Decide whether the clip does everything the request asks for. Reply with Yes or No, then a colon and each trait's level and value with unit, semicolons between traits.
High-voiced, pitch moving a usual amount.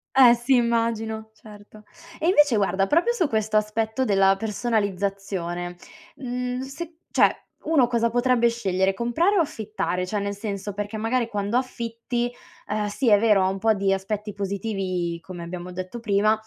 Yes: high, 215 Hz; average, 3.4 semitones